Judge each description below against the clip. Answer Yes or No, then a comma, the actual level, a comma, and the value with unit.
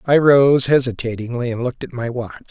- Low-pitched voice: Yes, low, 125 Hz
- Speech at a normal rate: Yes, average, 190 wpm